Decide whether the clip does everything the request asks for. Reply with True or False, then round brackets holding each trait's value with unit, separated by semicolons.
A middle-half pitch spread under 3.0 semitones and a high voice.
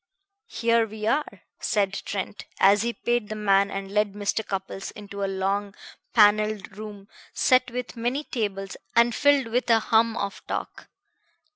True (2.6 semitones; 210 Hz)